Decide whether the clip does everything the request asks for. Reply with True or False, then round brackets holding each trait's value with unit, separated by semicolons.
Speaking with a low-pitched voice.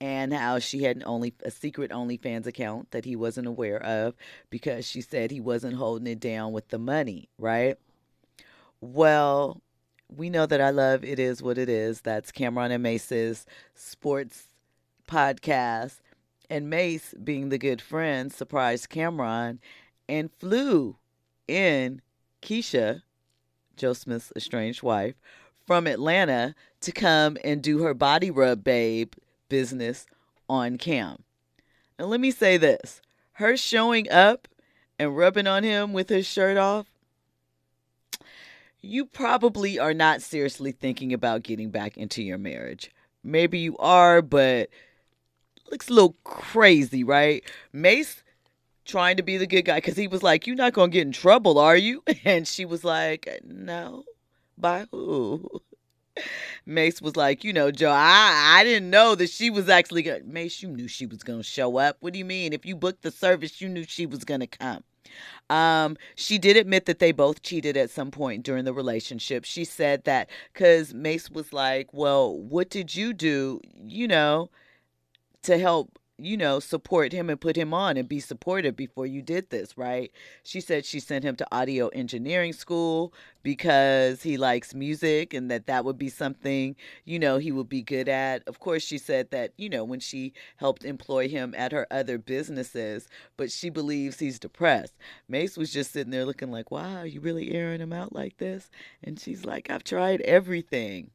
False (145 Hz)